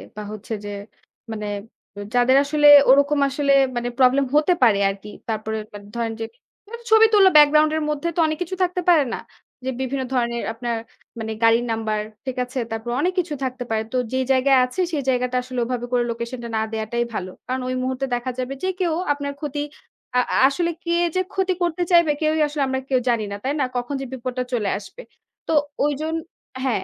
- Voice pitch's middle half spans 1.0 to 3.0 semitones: No, average, 4.2 semitones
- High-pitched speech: Yes, very high, 260 Hz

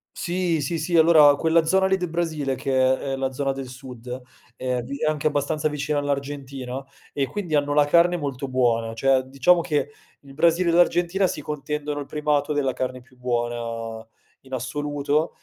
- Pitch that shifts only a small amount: No, average, 3.2 semitones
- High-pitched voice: No, medium, 145 Hz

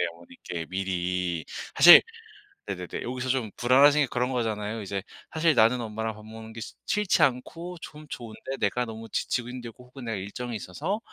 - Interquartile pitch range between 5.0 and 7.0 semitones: No, average, 3.7 semitones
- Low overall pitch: Yes, low, 115 Hz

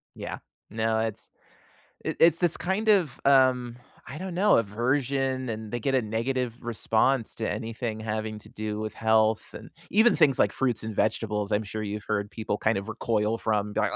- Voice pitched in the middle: No, low, 115 Hz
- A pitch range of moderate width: Yes, average, 3.6 semitones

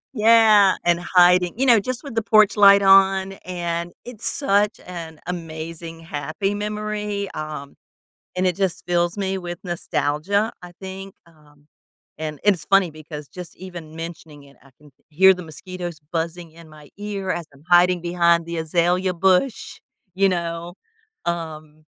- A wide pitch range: No, average, 3.1 semitones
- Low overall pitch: No, medium, 175 Hz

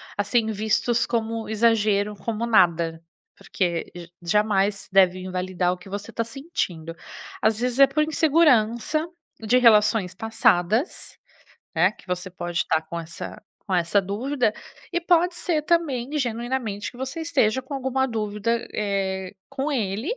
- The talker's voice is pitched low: No, high, 215 Hz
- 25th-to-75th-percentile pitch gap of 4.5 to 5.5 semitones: Yes, average, 5.1 semitones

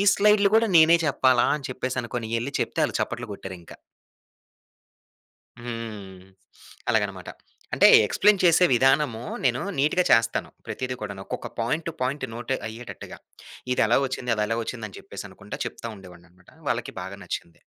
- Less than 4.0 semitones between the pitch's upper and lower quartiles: No, average, 4.7 semitones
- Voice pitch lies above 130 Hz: No, low, 120 Hz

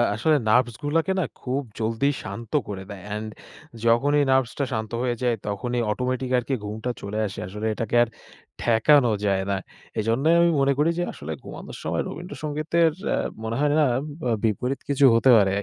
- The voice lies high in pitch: No, low, 120 Hz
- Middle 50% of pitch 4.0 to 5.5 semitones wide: Yes, average, 4.6 semitones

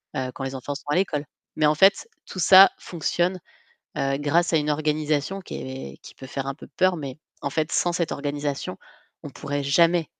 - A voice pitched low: No, medium, 150 Hz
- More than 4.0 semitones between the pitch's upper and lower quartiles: No, average, 3.6 semitones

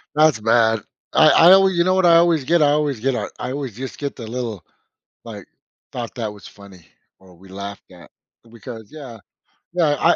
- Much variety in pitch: Yes, wide, 6.0 semitones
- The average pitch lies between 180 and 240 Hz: No, low, 125 Hz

